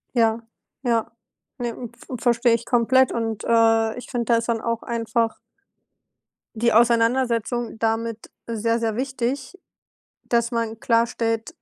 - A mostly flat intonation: Yes, narrow, 1.0 semitones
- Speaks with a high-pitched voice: Yes, high, 230 Hz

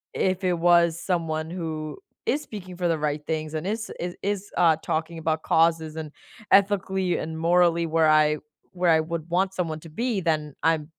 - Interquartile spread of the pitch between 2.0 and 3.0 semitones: Yes, narrow, 2.5 semitones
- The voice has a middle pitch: Yes, medium, 165 Hz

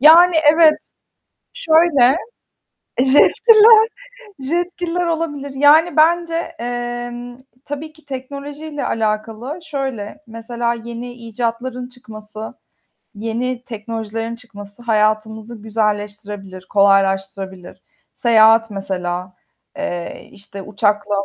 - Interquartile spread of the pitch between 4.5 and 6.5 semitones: Yes, wide, 5.5 semitones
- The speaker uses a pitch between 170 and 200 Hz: No, high, 235 Hz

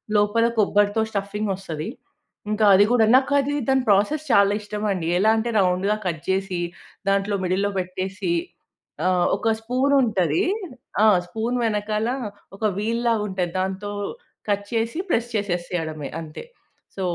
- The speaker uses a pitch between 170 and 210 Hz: Yes, high, 205 Hz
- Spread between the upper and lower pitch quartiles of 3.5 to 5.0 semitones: No, average, 3.0 semitones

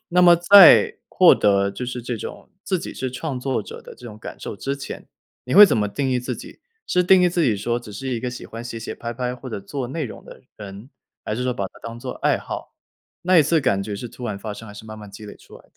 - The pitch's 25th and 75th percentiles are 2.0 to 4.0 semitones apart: No, average, 4.4 semitones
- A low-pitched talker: Yes, low, 125 Hz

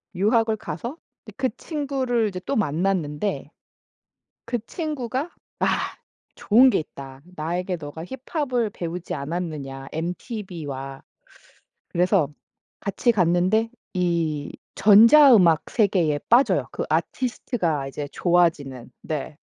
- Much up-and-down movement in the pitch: Yes, wide, 7.0 semitones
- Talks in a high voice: No, medium, 180 Hz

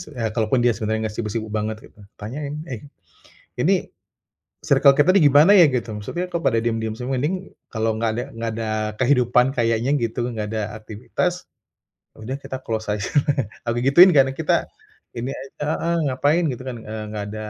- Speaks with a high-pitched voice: No, low, 120 Hz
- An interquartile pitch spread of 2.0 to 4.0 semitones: No, average, 4.5 semitones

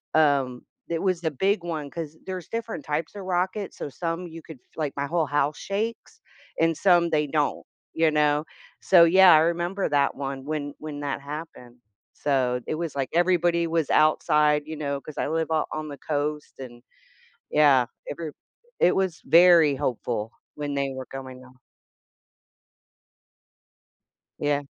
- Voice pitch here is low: No, medium, 155 Hz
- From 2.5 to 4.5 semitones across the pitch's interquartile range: Yes, average, 3.2 semitones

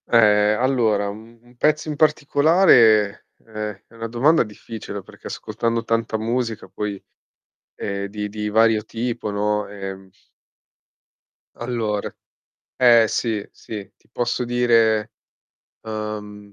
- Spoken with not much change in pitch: Yes, narrow, 2.2 semitones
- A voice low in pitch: Yes, low, 110 Hz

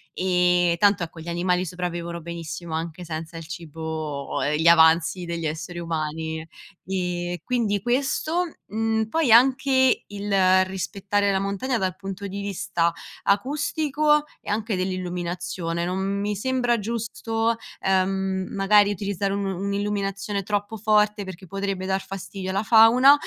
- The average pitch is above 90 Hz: Yes, high, 190 Hz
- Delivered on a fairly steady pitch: No, average, 3.3 semitones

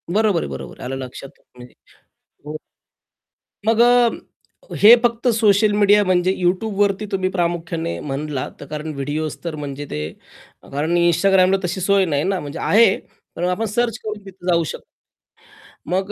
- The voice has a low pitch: No, medium, 185 Hz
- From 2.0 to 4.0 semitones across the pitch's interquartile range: No, average, 5.2 semitones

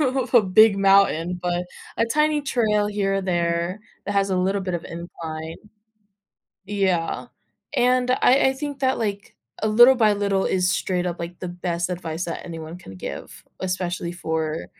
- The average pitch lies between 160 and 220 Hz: Yes, high, 190 Hz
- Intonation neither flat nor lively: Yes, average, 3.9 semitones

